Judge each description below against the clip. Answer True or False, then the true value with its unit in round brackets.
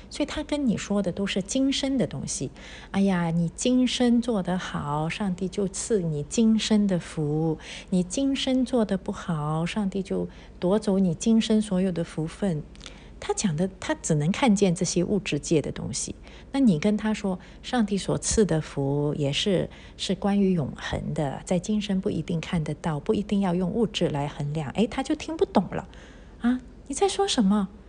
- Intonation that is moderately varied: True (4.7 semitones)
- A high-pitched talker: True (195 Hz)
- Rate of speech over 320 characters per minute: False (255 characters per minute)